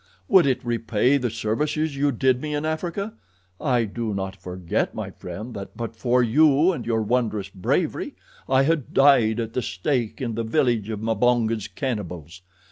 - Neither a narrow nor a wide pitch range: Yes, average, 4.1 semitones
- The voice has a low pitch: Yes, low, 120 Hz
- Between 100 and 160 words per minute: No, average, 170 wpm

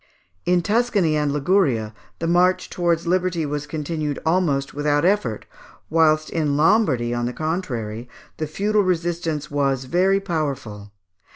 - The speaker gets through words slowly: Yes, slow, 130 wpm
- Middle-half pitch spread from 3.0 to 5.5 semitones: Yes, average, 4.1 semitones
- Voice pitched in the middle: Yes, medium, 155 Hz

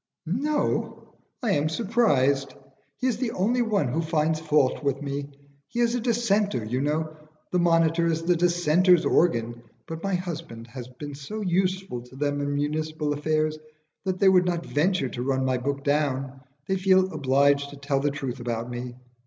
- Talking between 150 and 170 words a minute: No, average, 180 wpm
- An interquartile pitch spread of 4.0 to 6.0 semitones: Yes, average, 4.9 semitones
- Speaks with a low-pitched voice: No, medium, 155 Hz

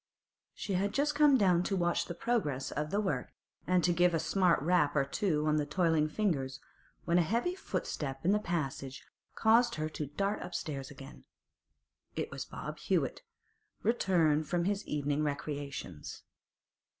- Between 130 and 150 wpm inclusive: No, average, 160 wpm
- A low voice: No, medium, 170 Hz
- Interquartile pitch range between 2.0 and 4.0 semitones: No, average, 5.0 semitones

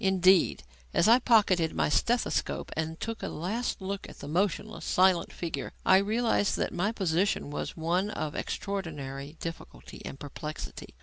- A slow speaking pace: No, average, 150 wpm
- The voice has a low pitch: No, medium, 185 Hz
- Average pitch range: Yes, average, 4.2 semitones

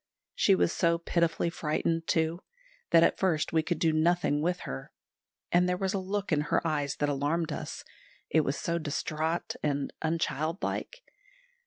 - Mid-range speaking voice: Yes, medium, 165 Hz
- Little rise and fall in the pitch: Yes, narrow, 2.3 semitones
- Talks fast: No, average, 165 wpm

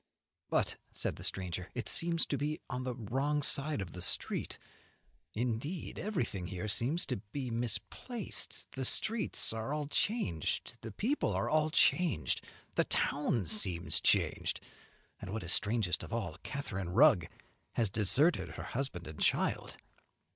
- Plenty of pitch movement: Yes, wide, 7.4 semitones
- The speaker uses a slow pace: No, average, 145 wpm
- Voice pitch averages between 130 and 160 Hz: No, low, 120 Hz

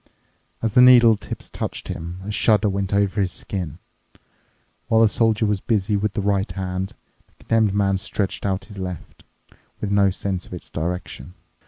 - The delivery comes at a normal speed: Yes, average, 175 wpm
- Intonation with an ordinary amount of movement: No, narrow, 2.2 semitones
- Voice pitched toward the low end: Yes, low, 100 Hz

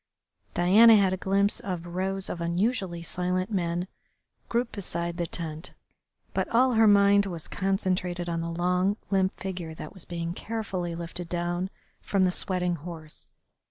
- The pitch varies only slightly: Yes, narrow, 2.3 semitones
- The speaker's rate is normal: Yes, average, 155 wpm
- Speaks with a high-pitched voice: No, medium, 180 Hz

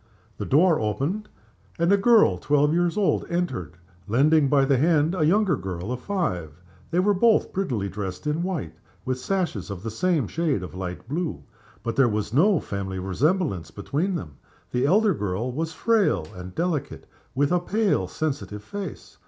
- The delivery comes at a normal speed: Yes, average, 170 wpm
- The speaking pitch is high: No, medium, 145 Hz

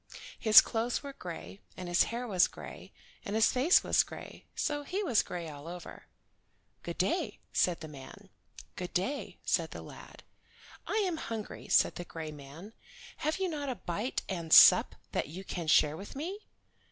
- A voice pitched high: Yes, high, 200 Hz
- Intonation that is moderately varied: No, wide, 8.0 semitones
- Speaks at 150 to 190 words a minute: Yes, average, 175 wpm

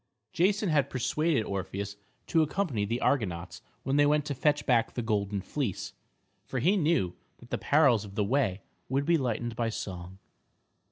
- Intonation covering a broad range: Yes, wide, 6.6 semitones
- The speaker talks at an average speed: Yes, average, 170 wpm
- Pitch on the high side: No, low, 125 Hz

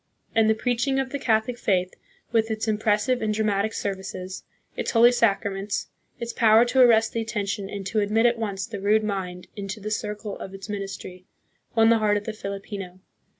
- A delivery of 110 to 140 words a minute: No, average, 190 wpm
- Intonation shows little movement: Yes, narrow, 2.3 semitones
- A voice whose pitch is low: No, high, 215 Hz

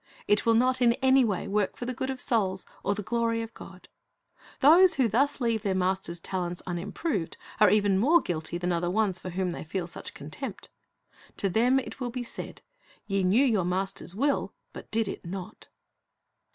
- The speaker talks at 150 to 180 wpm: No, average, 195 wpm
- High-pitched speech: Yes, high, 205 Hz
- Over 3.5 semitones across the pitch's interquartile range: Yes, average, 4.8 semitones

